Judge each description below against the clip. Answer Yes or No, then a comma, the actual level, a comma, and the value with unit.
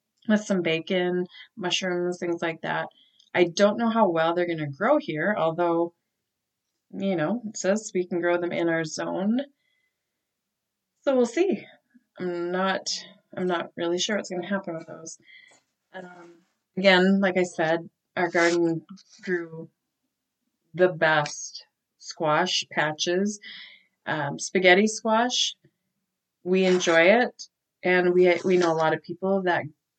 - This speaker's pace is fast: No, average, 145 wpm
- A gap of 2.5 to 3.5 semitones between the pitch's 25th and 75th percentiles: Yes, average, 2.9 semitones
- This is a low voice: No, medium, 180 Hz